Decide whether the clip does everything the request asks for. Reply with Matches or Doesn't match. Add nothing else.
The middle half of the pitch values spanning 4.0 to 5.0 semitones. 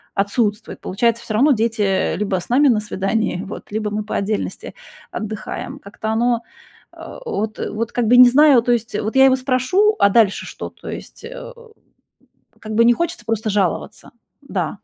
Doesn't match